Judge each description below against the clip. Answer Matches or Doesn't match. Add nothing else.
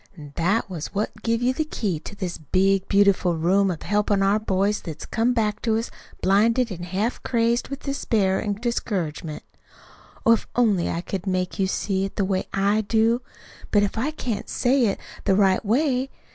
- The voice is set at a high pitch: Matches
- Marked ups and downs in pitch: Doesn't match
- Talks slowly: Doesn't match